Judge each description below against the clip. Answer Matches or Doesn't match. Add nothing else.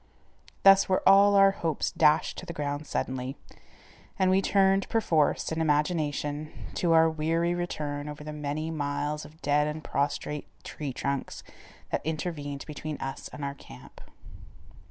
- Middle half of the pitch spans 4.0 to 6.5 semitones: Doesn't match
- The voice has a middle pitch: Matches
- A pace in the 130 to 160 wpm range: Matches